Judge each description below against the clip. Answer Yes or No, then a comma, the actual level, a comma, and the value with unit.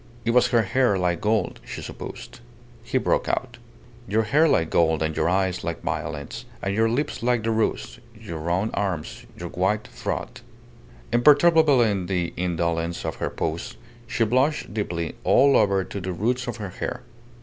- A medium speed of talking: Yes, average, 170 wpm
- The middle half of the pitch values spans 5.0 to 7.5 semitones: Yes, wide, 5.5 semitones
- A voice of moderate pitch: No, low, 100 Hz